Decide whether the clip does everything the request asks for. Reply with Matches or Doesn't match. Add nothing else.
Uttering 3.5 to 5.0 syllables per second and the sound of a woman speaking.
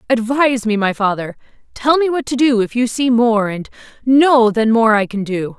Matches